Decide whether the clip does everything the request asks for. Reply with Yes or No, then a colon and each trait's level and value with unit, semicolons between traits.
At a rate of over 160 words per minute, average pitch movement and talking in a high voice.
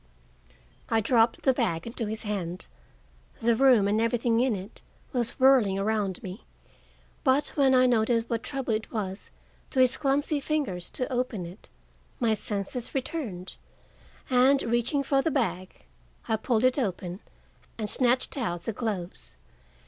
No: average, 150 wpm; average, 4.2 semitones; high, 230 Hz